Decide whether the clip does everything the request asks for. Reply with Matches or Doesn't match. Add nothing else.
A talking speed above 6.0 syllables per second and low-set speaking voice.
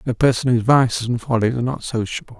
Matches